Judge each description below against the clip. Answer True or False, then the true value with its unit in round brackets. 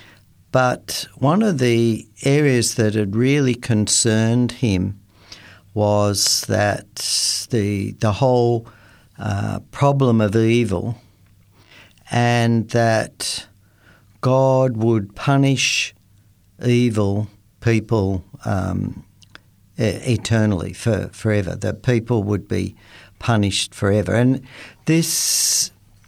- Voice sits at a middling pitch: False (110 Hz)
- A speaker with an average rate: False (85 wpm)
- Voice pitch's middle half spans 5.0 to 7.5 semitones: False (3.1 semitones)